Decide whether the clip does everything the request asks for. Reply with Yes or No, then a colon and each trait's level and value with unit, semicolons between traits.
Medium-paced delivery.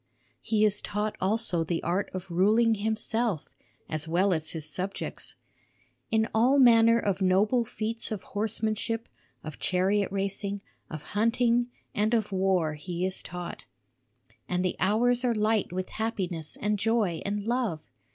Yes: average, 145 wpm